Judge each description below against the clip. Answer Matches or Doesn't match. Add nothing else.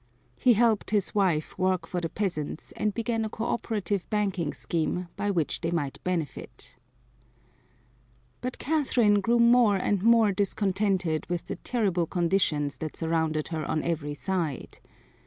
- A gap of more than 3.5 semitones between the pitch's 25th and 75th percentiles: Matches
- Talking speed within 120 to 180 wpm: Matches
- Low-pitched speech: Doesn't match